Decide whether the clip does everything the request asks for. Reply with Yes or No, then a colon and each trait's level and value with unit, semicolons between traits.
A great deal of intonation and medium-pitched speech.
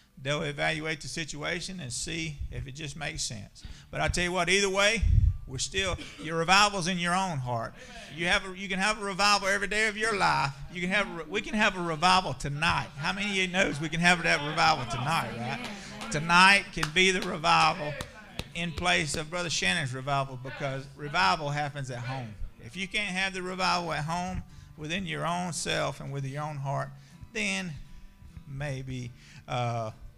No: average, 5.0 semitones; medium, 160 Hz